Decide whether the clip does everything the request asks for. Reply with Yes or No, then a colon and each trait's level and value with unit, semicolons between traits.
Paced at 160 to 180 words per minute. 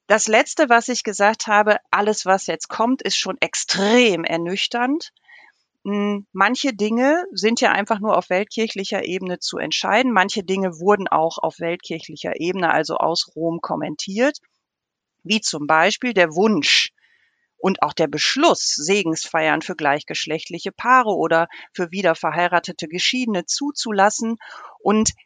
No: average, 135 wpm